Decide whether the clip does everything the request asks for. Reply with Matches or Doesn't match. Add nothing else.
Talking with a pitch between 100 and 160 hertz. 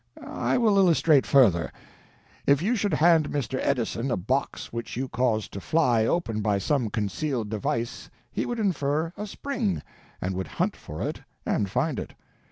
Matches